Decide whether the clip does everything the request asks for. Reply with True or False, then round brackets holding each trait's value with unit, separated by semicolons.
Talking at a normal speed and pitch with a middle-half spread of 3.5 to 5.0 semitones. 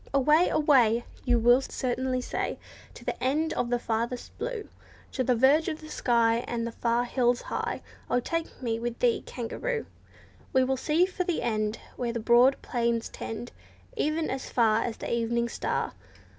False (180 wpm; 3.1 semitones)